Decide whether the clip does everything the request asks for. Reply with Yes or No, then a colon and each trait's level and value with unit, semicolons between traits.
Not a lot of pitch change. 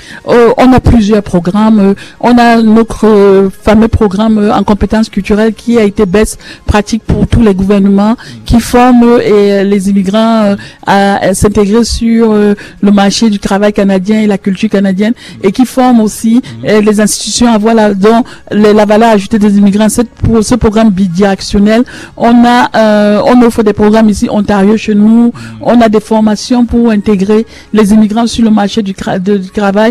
Yes: narrow, 1.9 semitones